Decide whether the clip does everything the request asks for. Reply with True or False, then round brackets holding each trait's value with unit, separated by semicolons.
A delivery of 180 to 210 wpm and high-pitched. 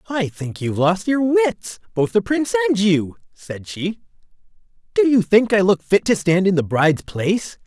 True (195 wpm; 200 Hz)